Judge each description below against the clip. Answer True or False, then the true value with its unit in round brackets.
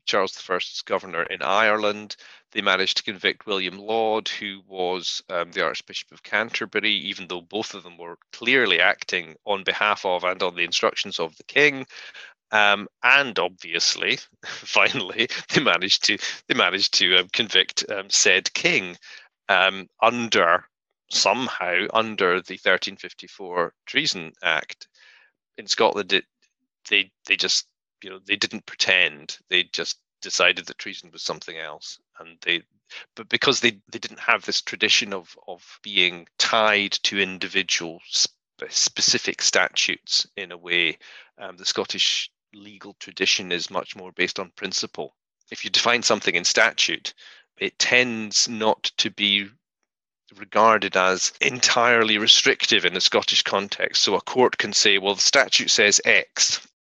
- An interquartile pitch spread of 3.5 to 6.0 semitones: False (3.1 semitones)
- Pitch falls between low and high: False (100 Hz)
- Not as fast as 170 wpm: True (150 wpm)